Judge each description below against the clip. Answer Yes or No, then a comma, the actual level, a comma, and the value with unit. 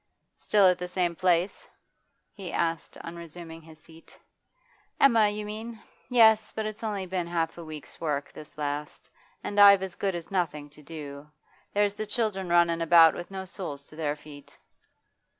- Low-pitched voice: No, medium, 175 Hz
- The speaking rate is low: No, average, 170 wpm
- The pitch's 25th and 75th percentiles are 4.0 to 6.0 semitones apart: Yes, average, 4.4 semitones